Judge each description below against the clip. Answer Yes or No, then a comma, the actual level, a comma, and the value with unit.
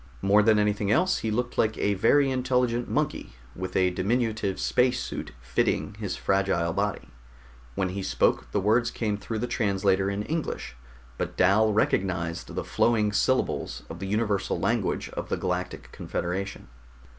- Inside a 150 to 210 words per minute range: Yes, average, 155 wpm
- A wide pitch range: No, average, 3.4 semitones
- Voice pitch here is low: Yes, low, 105 Hz